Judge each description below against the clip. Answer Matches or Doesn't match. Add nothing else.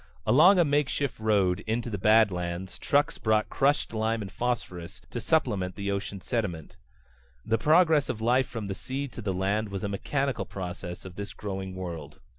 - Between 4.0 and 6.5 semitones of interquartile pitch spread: Matches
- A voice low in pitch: Matches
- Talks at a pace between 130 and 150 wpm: Doesn't match